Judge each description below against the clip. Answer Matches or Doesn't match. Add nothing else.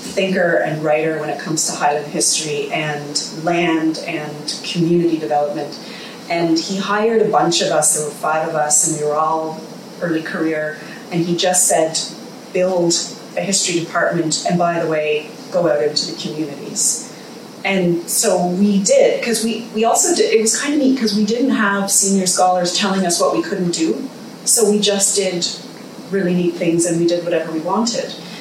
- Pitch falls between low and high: Matches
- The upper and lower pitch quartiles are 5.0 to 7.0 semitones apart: Matches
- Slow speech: Doesn't match